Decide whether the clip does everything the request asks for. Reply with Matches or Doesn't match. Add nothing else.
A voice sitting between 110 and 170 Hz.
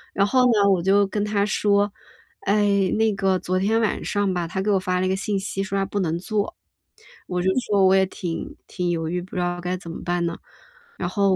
Doesn't match